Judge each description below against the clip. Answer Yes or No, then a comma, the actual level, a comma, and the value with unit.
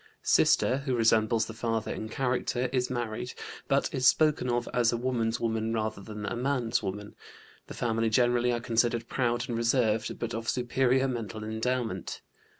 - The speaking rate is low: No, average, 165 wpm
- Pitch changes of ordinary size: No, narrow, 1.9 semitones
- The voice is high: No, low, 120 Hz